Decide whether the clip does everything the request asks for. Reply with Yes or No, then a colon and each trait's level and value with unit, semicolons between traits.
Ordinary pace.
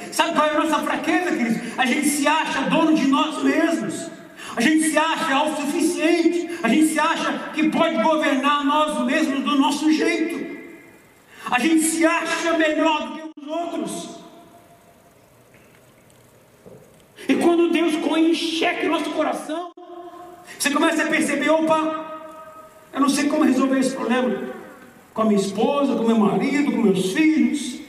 Yes: average, 155 wpm